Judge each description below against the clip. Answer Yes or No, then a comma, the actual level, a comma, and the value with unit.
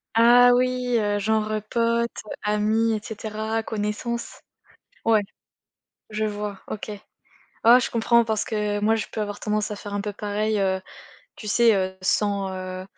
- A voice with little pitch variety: Yes, narrow, 1.8 semitones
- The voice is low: No, high, 215 Hz